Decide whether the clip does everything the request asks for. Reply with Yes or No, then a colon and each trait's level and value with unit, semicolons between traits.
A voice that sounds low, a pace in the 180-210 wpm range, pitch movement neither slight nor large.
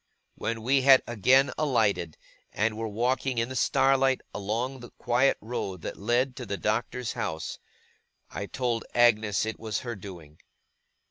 No: low, 115 Hz; average, 150 wpm; average, 3.5 semitones